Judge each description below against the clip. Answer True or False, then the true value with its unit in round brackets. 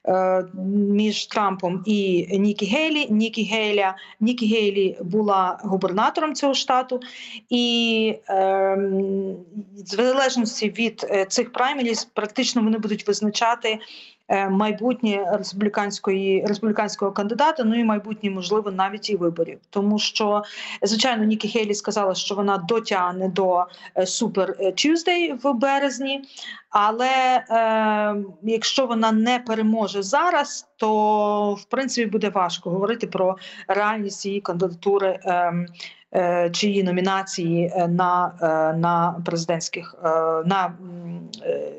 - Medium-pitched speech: False (210 Hz)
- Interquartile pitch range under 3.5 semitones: True (3.1 semitones)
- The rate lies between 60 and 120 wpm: True (110 wpm)